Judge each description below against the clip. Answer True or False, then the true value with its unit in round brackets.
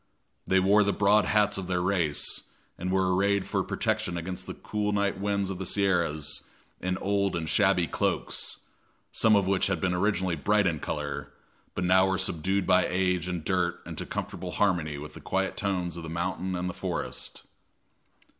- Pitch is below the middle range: True (95 Hz)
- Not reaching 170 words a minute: False (185 wpm)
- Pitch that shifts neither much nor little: False (2.1 semitones)